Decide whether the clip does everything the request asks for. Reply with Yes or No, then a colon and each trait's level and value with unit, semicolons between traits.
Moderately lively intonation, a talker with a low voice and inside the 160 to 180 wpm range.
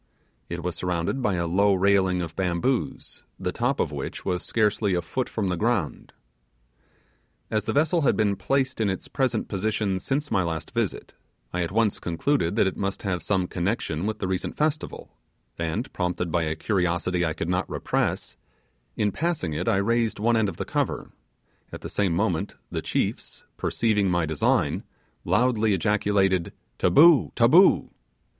Yes: average, 4.1 semitones; low, 100 Hz; average, 170 wpm